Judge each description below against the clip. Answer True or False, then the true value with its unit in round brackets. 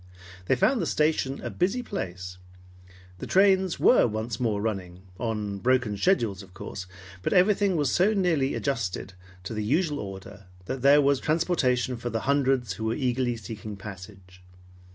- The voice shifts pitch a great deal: True (7.1 semitones)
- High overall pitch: False (120 Hz)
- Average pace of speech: True (160 wpm)